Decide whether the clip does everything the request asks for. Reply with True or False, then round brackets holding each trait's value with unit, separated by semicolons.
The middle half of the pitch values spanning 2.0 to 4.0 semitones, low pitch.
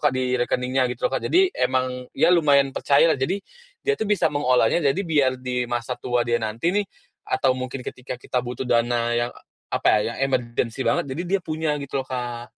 True (3.2 semitones; 130 Hz)